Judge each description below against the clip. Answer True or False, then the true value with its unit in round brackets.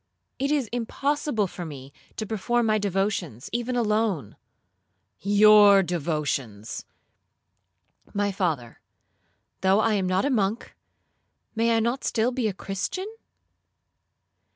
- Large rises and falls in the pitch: False (4.1 semitones)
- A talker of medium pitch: False (205 Hz)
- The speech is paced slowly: True (105 wpm)